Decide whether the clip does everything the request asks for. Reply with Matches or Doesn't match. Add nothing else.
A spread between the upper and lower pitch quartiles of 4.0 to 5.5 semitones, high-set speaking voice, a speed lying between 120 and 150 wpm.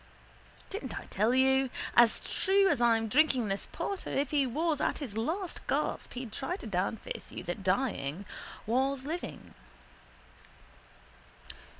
Matches